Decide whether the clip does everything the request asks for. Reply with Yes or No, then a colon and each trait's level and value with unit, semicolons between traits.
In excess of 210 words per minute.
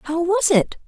No: fast, 205 wpm